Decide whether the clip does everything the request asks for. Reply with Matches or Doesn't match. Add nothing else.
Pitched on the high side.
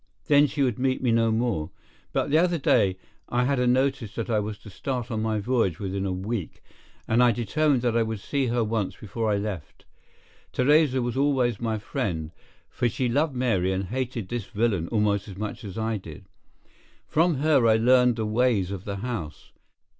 Doesn't match